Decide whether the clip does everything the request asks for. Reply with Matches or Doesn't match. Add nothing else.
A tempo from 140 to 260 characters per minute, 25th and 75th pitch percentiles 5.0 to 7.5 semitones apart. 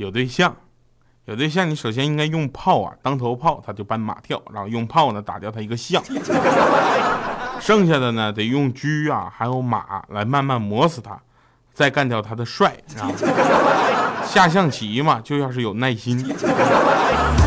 Matches